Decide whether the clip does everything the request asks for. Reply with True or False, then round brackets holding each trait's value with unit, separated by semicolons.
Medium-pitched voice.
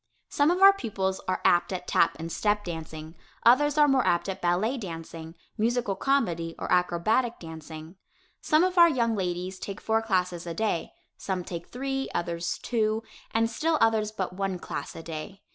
False (195 Hz)